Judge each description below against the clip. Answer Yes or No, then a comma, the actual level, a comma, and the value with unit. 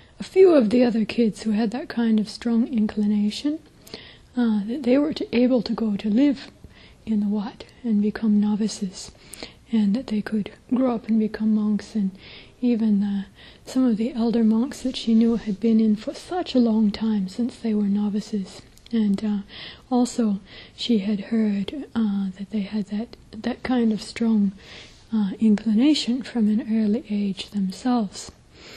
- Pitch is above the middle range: Yes, high, 220 Hz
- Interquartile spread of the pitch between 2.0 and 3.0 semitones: Yes, narrow, 2.4 semitones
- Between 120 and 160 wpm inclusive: No, average, 175 wpm